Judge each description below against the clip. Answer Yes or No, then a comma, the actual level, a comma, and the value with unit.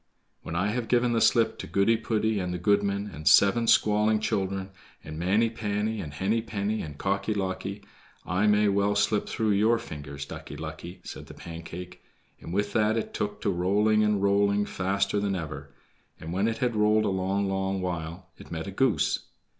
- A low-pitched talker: Yes, low, 100 Hz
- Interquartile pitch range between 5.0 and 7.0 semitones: No, average, 2.8 semitones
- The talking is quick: No, average, 190 wpm